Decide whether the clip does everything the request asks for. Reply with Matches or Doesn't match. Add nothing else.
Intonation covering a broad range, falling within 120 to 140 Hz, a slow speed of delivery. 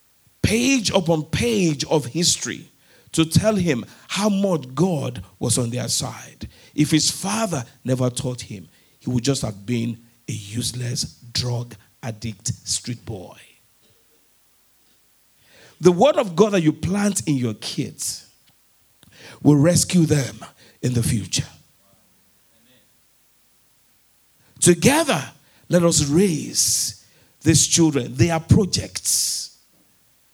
Matches